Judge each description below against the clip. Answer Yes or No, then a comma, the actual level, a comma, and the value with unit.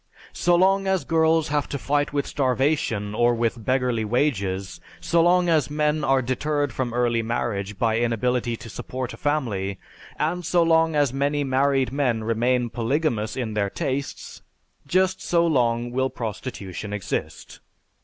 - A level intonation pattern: No, average, 4.5 semitones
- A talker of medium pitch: No, low, 130 Hz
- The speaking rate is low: No, average, 155 wpm